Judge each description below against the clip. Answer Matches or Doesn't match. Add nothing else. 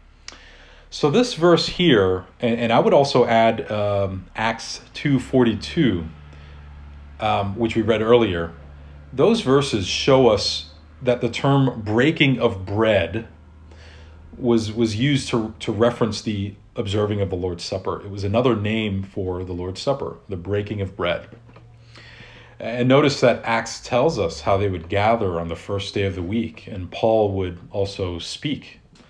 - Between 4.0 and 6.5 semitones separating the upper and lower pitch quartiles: Matches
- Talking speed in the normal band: Matches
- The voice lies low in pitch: Matches